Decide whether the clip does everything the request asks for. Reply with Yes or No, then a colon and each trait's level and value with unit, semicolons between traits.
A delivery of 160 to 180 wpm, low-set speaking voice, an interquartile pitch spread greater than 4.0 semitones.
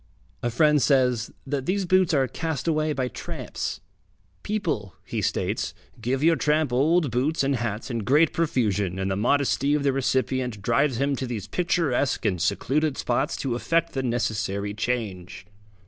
Yes: average, 165 wpm; low, 130 Hz; average, 4.7 semitones